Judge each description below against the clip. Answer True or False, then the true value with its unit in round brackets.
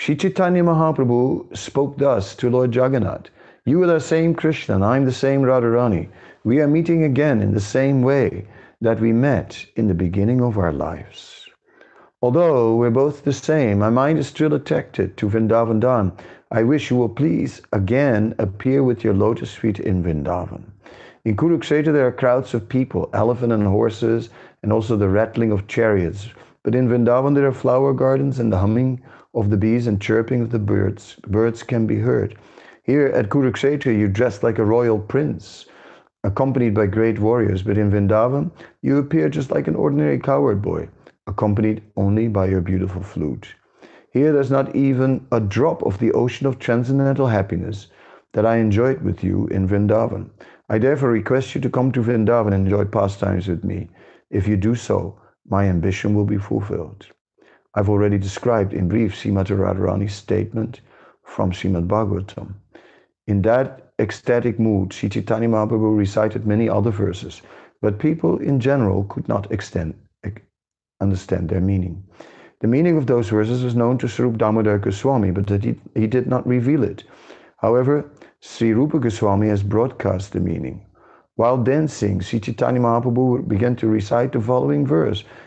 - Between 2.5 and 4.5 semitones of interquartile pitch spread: True (4.2 semitones)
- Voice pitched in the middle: False (115 Hz)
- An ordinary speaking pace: True (170 wpm)